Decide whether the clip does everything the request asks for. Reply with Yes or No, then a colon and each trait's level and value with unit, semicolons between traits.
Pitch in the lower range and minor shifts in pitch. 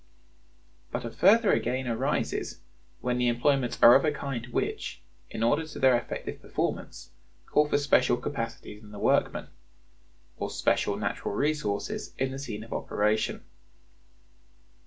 No: low, 125 Hz; average, 3.7 semitones